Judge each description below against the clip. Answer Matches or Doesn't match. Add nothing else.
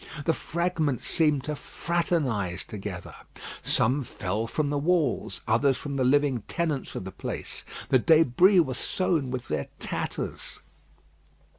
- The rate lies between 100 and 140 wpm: Matches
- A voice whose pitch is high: Doesn't match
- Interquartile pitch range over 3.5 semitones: Matches